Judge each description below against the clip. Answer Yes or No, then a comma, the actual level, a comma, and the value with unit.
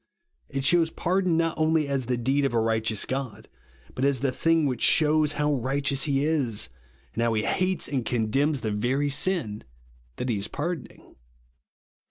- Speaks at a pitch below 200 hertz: Yes, medium, 140 Hz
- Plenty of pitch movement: No, average, 4.7 semitones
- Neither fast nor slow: Yes, average, 175 wpm